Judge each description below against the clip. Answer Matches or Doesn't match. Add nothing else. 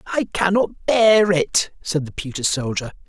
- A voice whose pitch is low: Doesn't match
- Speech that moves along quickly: Doesn't match